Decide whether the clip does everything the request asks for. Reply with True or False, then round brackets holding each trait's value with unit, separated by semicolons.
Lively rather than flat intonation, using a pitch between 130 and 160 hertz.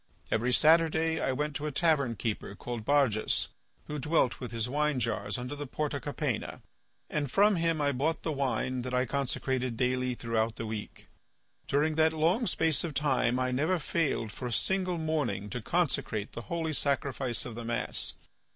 False (4.3 semitones; 140 Hz)